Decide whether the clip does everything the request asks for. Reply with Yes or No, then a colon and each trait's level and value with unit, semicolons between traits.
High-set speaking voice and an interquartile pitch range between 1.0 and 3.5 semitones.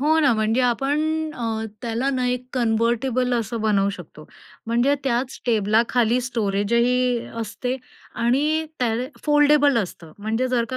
Yes: high, 240 Hz; narrow, 2.5 semitones